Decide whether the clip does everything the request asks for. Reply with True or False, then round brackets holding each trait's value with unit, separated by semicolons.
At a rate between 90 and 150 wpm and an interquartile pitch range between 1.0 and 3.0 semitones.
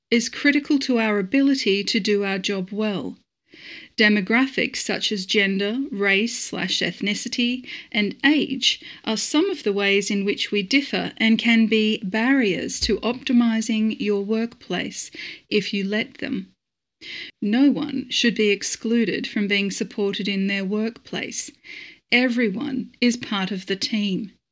False (140 wpm; 4.2 semitones)